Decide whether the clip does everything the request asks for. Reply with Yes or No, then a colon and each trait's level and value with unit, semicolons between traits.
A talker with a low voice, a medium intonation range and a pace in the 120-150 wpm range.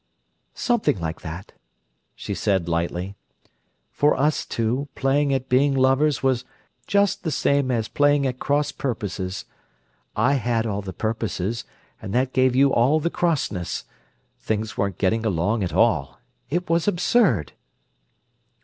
No: low, 125 Hz; wide, 6.2 semitones; average, 140 wpm